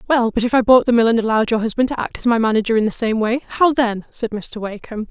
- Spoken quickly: Yes, fast, 295 wpm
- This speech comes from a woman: Yes, female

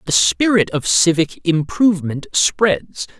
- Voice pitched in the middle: Yes, medium, 170 Hz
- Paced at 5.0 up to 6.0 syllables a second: No, 3.8 syllables/s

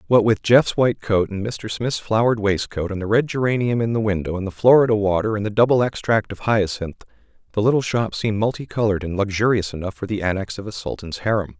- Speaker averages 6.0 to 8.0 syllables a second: Yes, 6.2 syllables/s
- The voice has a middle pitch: No, low, 105 Hz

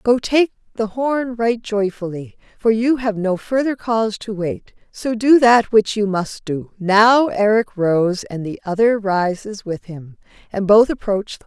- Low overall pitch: No, high, 210 Hz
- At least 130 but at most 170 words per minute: No, average, 185 wpm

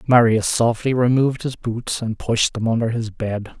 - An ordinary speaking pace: Yes, average, 185 wpm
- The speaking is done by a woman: No, male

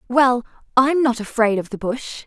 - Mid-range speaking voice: No, high, 245 Hz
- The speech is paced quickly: No, average, 185 wpm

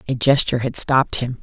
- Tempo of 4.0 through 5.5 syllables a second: No, 6.4 syllables/s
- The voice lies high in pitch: No, low, 125 Hz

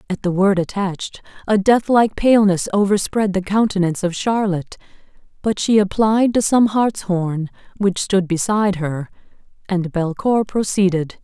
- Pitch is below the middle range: No, high, 195 Hz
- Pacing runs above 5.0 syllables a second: No, 4.8 syllables/s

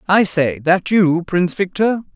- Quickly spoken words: No, average, 165 wpm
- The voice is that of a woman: Yes, female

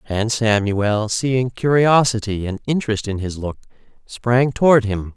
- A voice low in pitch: Yes, low, 115 Hz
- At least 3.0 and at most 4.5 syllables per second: Yes, 4.3 syllables/s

